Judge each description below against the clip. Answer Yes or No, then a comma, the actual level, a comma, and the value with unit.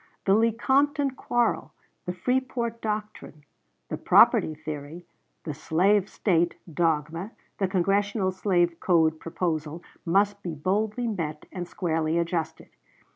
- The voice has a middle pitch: Yes, medium, 180 Hz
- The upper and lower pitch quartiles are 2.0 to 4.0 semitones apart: No, average, 4.6 semitones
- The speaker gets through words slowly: Yes, slow, 115 wpm